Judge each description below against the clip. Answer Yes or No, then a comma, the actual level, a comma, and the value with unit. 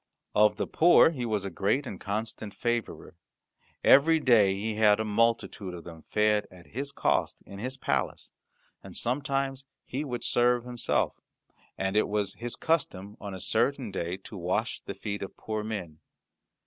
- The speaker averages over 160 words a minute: Yes, average, 170 wpm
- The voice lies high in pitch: No, low, 110 Hz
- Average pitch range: Yes, average, 3.8 semitones